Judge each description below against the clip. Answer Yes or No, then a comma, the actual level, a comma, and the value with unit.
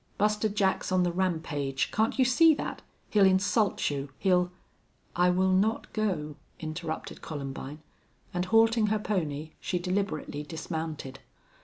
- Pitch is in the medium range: Yes, medium, 180 Hz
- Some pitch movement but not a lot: Yes, average, 5.0 semitones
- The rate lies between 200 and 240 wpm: No, average, 140 wpm